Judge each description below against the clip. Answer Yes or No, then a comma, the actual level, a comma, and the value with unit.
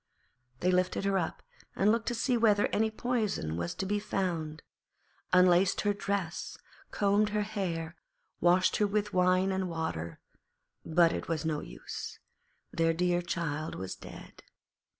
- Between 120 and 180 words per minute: Yes, average, 150 wpm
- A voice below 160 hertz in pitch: No, medium, 185 Hz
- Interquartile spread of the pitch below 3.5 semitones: No, average, 3.8 semitones